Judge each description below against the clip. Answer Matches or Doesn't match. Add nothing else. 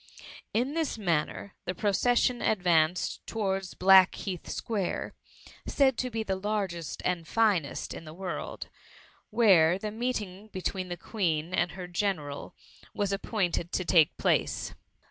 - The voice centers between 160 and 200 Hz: Matches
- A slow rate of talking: Doesn't match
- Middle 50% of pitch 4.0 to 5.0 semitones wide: Doesn't match